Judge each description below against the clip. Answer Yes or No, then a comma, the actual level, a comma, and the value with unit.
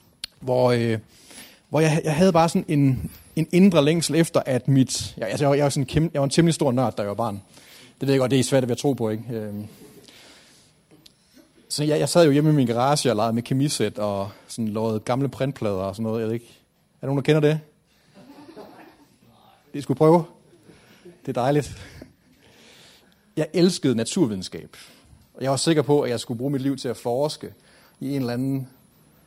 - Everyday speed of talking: Yes, average, 205 wpm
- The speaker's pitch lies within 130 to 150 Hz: Yes, medium, 140 Hz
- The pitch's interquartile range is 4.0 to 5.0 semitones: Yes, average, 4.6 semitones